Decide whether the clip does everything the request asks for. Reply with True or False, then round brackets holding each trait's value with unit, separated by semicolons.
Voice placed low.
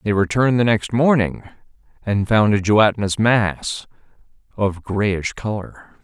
True (105 Hz)